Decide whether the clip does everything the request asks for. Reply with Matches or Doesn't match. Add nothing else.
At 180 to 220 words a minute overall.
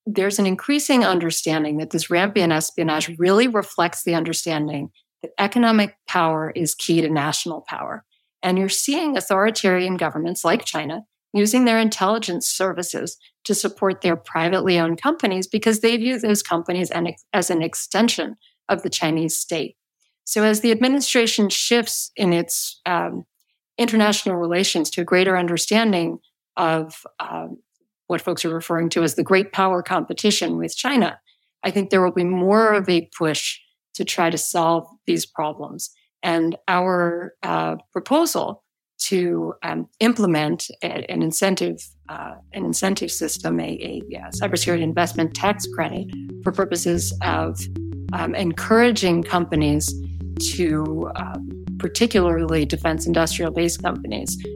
Doesn't match